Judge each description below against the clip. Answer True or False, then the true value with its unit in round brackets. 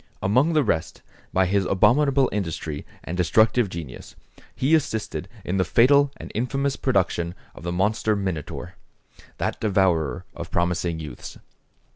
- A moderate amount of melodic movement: False (6.3 semitones)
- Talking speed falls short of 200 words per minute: True (135 wpm)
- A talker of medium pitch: False (95 Hz)